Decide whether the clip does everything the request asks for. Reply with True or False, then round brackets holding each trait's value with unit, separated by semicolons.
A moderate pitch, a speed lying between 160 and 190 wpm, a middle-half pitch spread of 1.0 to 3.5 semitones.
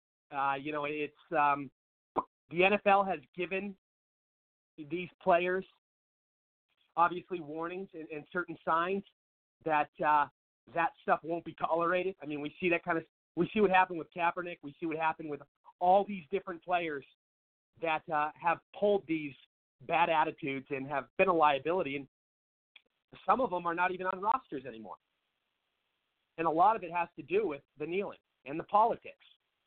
False (165 Hz; 165 wpm; 4.0 semitones)